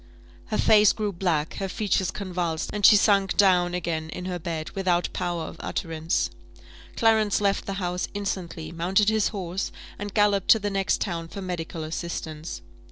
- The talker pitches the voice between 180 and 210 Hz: Yes, medium, 185 Hz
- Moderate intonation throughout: Yes, average, 3.2 semitones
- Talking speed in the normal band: Yes, average, 165 wpm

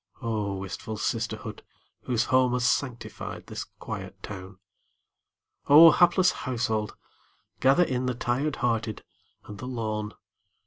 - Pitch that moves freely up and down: No, average, 3.2 semitones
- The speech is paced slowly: Yes, slow, 120 wpm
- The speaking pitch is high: No, low, 120 Hz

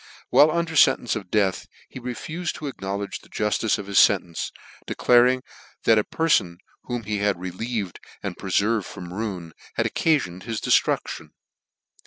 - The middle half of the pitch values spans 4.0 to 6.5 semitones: Yes, average, 4.4 semitones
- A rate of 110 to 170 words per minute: Yes, average, 160 wpm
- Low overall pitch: Yes, low, 105 Hz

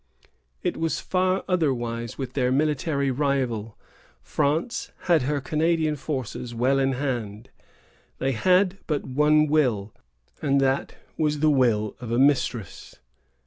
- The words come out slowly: Yes, slow, 130 wpm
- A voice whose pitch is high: No, medium, 140 Hz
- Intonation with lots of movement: No, average, 3.7 semitones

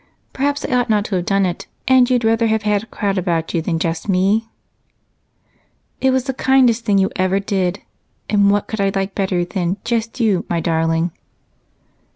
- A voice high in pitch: Yes, high, 200 Hz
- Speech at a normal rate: Yes, average, 190 wpm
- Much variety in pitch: No, average, 3.9 semitones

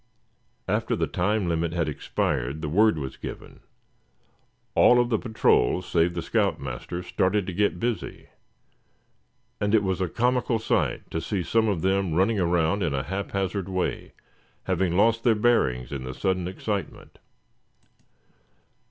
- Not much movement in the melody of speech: No, average, 4.2 semitones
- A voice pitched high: No, very low, 95 Hz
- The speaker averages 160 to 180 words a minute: No, average, 150 wpm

